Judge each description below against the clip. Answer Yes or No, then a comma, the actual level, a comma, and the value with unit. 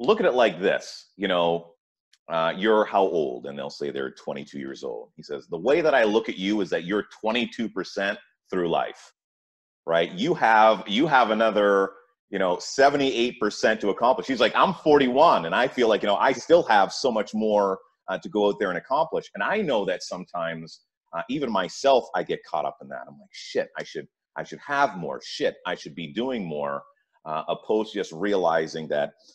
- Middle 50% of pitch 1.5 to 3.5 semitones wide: No, average, 5.1 semitones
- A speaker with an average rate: No, fast, 215 wpm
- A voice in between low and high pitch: No, very low, 95 Hz